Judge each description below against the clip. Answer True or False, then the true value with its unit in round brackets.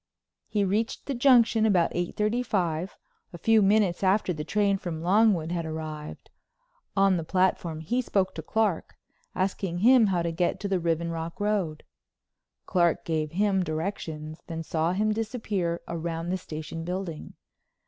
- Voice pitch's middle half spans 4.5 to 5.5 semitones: False (4.0 semitones)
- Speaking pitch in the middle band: True (180 Hz)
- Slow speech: False (160 wpm)